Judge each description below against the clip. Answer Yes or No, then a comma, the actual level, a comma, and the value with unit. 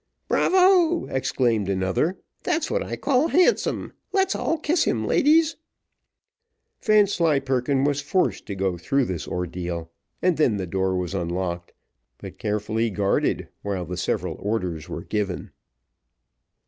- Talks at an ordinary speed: No, slow, 130 wpm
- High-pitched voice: No, low, 110 Hz